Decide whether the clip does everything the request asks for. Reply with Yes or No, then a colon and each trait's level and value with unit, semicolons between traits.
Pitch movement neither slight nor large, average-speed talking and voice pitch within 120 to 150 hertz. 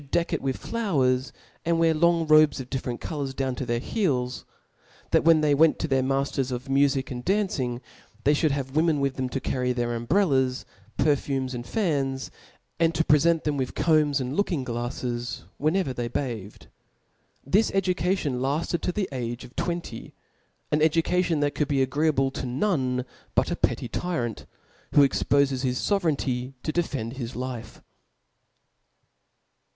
Yes: average, 4.1 semitones; average, 170 wpm; medium, 140 Hz